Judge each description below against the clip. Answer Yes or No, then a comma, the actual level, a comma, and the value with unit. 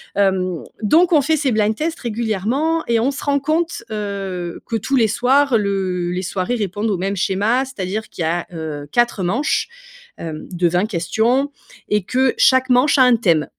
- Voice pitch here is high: Yes, high, 215 Hz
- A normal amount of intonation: No, wide, 6.0 semitones